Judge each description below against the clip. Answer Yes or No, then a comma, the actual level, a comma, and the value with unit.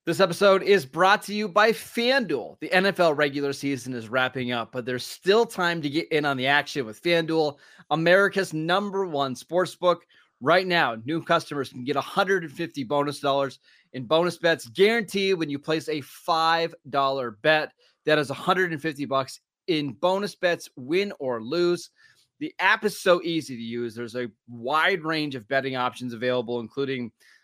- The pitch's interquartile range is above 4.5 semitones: Yes, average, 5.0 semitones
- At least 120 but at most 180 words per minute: Yes, average, 165 wpm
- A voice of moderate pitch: Yes, medium, 155 Hz